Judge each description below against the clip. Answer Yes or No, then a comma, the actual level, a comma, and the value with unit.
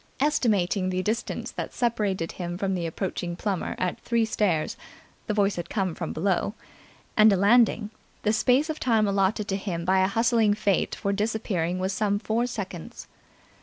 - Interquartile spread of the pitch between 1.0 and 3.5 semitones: Yes, average, 3.1 semitones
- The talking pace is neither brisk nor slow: Yes, average, 170 wpm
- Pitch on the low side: No, high, 200 Hz